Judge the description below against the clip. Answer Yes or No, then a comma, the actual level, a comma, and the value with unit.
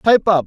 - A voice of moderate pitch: Yes, medium, 180 Hz